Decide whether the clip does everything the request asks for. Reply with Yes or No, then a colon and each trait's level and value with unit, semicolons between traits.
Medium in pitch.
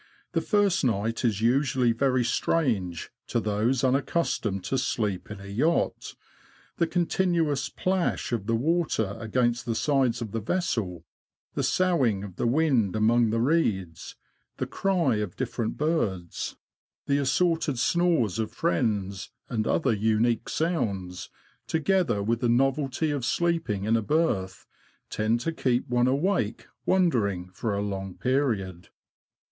No: low, 120 Hz